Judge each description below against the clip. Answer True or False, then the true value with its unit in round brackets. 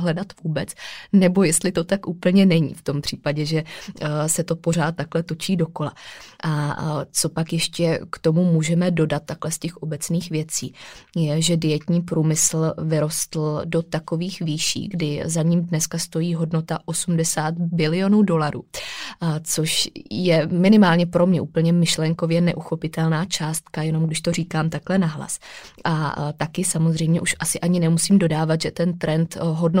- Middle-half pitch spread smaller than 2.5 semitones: True (1.7 semitones)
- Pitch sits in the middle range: True (165 Hz)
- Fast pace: False (150 wpm)